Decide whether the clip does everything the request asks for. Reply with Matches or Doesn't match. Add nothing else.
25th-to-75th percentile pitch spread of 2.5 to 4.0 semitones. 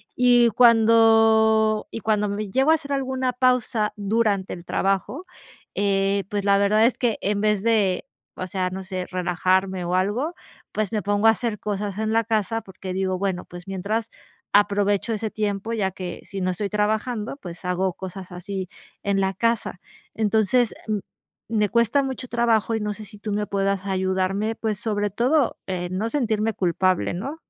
Matches